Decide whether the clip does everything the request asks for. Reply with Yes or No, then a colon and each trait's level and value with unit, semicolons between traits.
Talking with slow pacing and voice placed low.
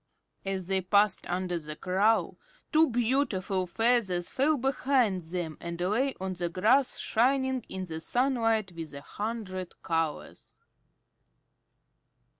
No: slow, 120 wpm; high, 195 Hz